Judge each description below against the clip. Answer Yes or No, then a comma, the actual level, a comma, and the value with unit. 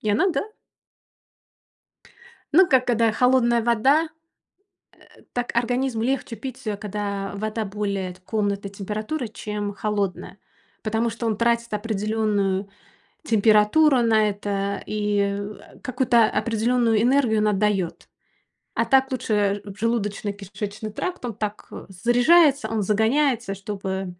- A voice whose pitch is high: Yes, high, 215 Hz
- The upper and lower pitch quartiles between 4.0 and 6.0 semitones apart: No, average, 2.9 semitones